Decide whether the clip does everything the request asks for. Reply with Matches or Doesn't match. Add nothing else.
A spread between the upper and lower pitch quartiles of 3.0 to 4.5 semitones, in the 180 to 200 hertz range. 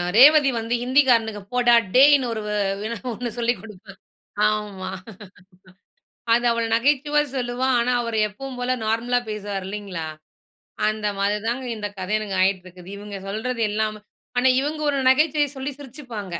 Doesn't match